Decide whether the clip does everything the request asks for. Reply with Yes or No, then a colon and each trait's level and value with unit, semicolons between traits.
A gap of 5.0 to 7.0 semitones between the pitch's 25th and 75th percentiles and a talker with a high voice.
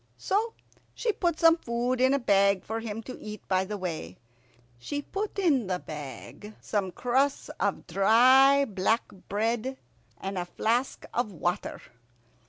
Yes: wide, 5.6 semitones; high, 225 Hz